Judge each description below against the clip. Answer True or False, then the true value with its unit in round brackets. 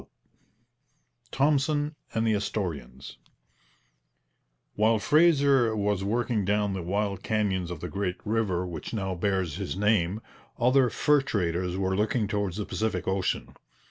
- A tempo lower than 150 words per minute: True (140 wpm)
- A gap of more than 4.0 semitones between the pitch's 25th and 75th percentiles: False (3.5 semitones)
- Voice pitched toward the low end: True (105 Hz)